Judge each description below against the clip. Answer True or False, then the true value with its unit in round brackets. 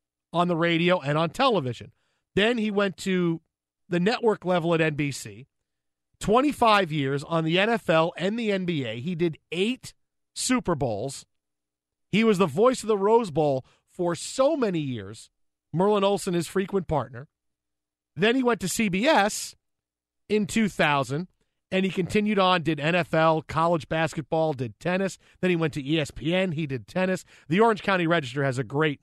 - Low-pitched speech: False (170 Hz)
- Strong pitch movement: True (5.8 semitones)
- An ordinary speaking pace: True (160 wpm)